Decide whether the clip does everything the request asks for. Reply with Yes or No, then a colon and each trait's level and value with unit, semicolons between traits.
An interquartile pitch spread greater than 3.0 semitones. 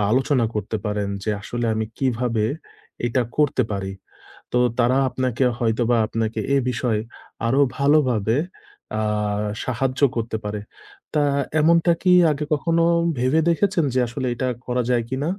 Yes: average, 3.8 semitones